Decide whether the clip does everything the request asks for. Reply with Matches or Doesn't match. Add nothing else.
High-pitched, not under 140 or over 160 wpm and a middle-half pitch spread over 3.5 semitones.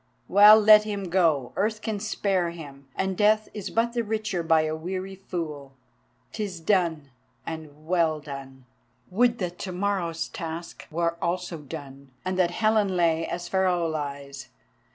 Doesn't match